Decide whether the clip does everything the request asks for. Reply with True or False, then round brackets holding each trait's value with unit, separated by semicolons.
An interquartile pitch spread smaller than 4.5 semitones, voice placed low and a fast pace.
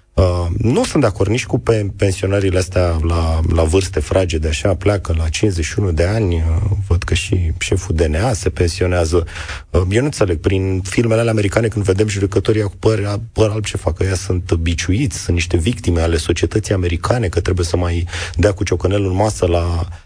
True (3.3 semitones; 95 Hz; 195 wpm)